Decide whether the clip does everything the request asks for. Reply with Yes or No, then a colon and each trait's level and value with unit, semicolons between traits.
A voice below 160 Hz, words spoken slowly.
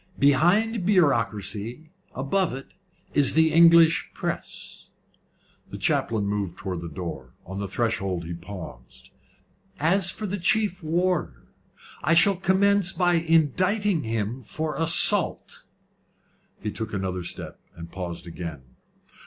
Yes: medium, 140 Hz; slow, 120 wpm